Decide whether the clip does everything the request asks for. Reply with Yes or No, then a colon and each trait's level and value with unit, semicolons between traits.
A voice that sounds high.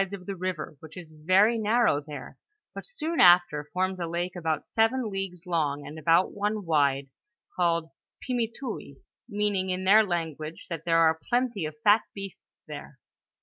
No: medium, 180 Hz